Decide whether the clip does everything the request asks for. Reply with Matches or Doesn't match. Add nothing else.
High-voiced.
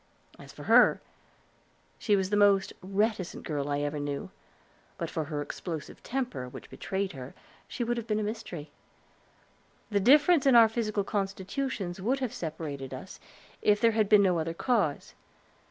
Matches